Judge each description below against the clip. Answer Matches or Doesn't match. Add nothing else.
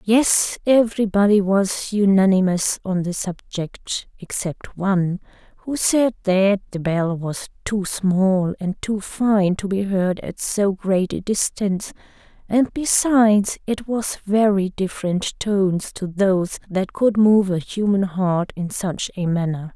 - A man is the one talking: Doesn't match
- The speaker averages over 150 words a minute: Doesn't match